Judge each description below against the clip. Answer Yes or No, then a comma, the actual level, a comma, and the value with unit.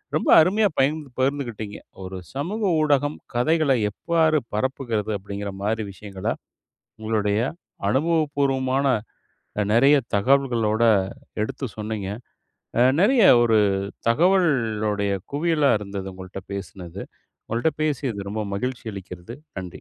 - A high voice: No, low, 120 Hz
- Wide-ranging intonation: Yes, wide, 6.0 semitones